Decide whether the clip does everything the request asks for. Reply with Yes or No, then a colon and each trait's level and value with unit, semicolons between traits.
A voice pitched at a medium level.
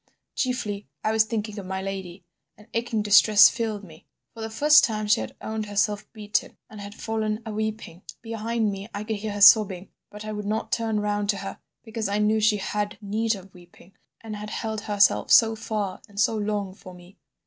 No: high, 210 Hz